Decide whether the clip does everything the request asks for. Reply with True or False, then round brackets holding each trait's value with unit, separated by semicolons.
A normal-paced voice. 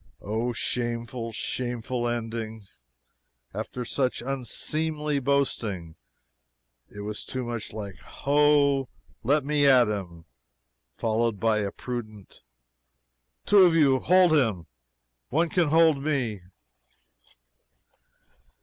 False (100 wpm)